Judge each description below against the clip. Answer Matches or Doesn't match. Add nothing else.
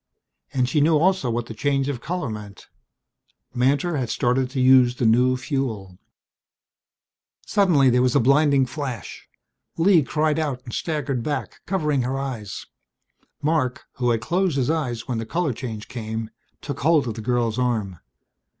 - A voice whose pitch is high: Doesn't match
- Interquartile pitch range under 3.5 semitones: Doesn't match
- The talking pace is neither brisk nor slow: Matches